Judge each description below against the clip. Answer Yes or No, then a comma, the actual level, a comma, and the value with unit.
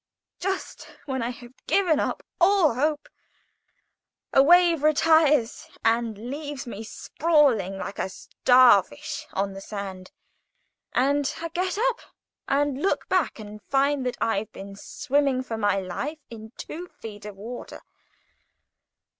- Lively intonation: Yes, wide, 6.0 semitones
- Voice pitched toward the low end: No, very high, 260 Hz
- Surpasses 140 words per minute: No, slow, 135 wpm